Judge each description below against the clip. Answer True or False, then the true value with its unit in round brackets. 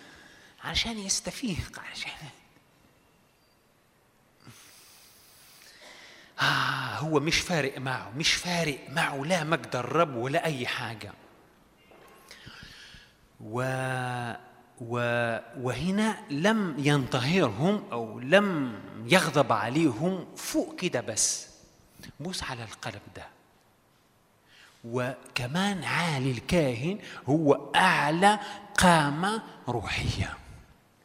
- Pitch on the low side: False (145 Hz)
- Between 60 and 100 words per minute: True (75 wpm)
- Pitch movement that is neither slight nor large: False (6.2 semitones)